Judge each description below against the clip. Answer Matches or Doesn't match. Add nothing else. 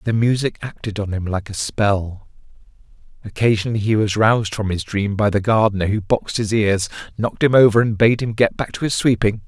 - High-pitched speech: Doesn't match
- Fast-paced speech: Matches